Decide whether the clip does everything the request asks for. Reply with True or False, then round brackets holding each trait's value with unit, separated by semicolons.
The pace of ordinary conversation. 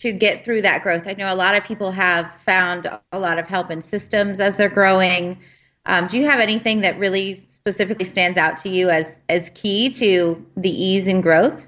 False (215 wpm)